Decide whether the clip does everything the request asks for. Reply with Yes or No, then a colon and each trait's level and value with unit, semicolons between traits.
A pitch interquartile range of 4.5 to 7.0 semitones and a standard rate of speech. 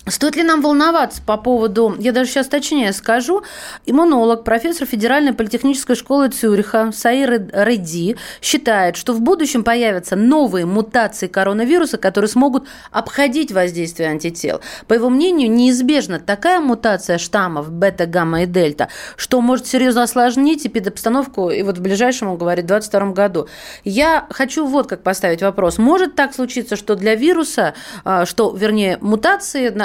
Yes: wide, 5.6 semitones; average, 145 wpm